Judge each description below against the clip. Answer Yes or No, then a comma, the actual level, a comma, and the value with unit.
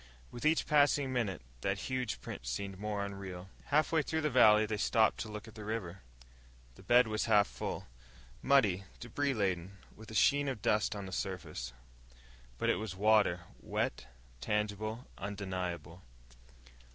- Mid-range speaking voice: No, low, 105 Hz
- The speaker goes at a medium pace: Yes, average, 155 wpm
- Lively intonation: No, average, 3.8 semitones